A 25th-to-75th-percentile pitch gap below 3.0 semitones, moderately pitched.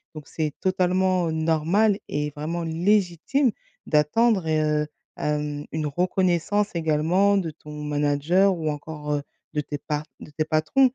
No: average, 3.7 semitones; medium, 160 Hz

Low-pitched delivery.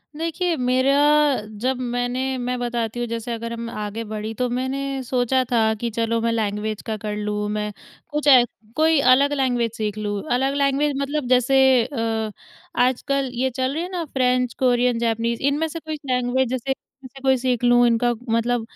No: high, 245 Hz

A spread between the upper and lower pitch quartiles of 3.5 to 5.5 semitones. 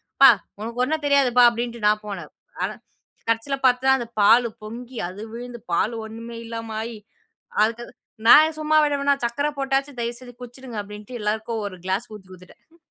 No: average, 3.1 semitones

